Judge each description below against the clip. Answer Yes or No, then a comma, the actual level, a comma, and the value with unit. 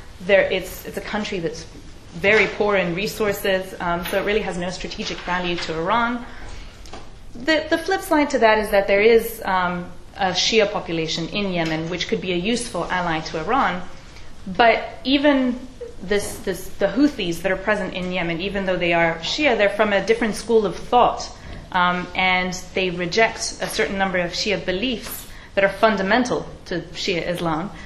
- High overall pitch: Yes, high, 195 Hz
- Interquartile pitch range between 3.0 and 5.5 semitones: Yes, average, 3.7 semitones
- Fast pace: No, average, 180 wpm